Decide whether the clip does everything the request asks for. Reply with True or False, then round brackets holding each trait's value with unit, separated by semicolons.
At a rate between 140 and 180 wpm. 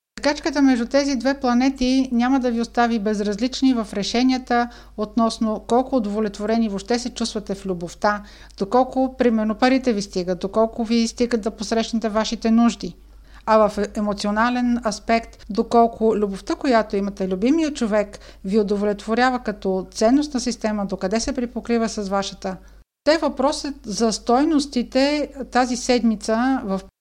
False (130 wpm)